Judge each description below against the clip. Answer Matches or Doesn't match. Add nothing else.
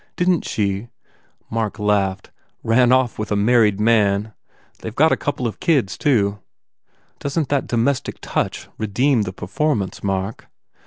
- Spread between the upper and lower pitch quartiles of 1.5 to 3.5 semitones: Doesn't match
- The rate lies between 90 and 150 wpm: Doesn't match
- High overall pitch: Doesn't match